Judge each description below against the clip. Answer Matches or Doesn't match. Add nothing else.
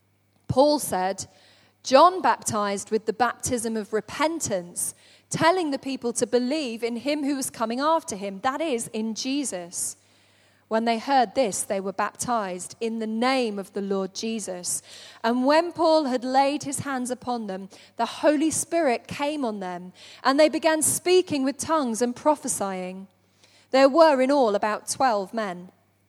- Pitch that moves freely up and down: Matches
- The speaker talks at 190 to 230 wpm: Doesn't match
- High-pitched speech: Matches